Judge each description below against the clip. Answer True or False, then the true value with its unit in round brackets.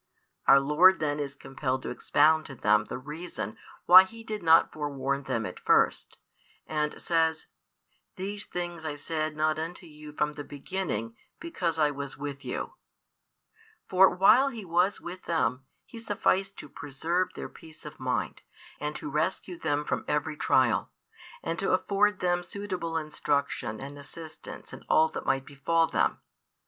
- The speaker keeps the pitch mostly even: False (3.9 semitones)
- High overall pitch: False (155 Hz)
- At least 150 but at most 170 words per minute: True (160 wpm)